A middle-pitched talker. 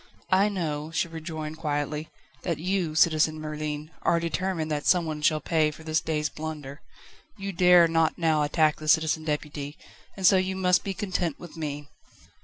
Yes: medium, 160 Hz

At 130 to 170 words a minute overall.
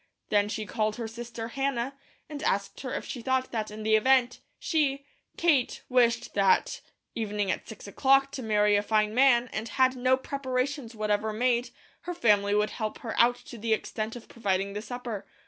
No: average, 190 wpm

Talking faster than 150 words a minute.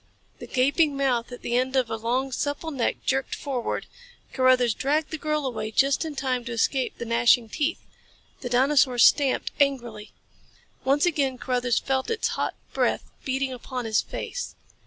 Yes: average, 165 wpm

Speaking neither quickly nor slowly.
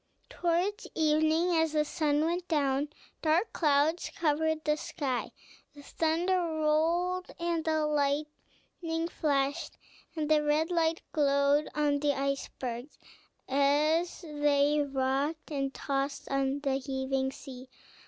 No: slow, 120 wpm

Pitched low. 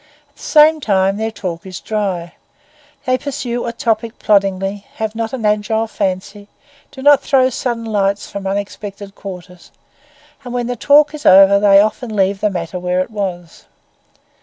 No: high, 205 Hz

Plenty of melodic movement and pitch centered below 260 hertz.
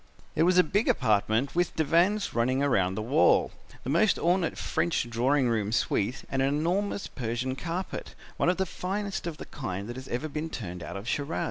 Yes: wide, 6.7 semitones; medium, 140 Hz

